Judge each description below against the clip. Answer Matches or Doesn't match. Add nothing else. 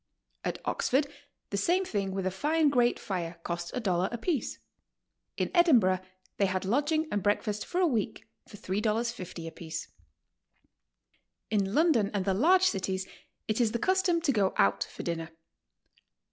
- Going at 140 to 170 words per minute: Matches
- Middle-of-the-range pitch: Doesn't match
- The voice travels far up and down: Matches